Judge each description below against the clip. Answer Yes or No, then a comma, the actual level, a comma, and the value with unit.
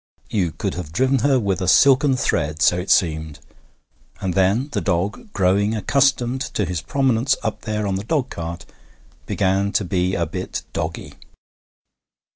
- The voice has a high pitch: No, low, 100 Hz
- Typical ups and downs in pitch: No, wide, 6.0 semitones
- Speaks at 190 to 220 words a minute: No, average, 155 wpm